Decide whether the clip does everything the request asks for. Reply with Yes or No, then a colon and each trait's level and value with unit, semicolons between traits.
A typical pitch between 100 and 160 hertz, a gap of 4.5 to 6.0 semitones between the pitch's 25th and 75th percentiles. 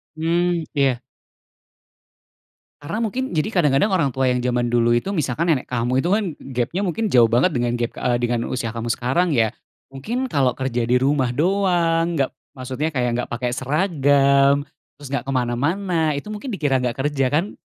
Yes: medium, 140 Hz; wide, 5.4 semitones